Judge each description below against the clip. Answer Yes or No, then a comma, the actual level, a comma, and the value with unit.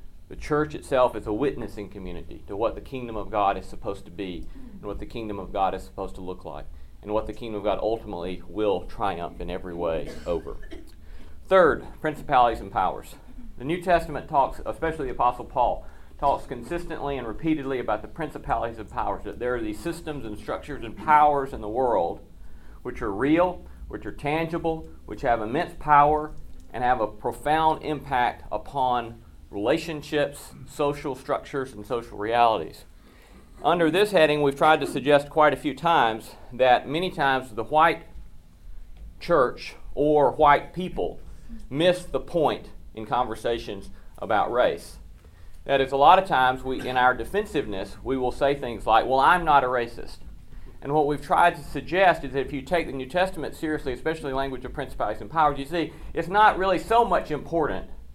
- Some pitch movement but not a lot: No, wide, 6.4 semitones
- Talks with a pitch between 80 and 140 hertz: Yes, low, 135 Hz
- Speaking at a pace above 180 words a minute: No, average, 175 wpm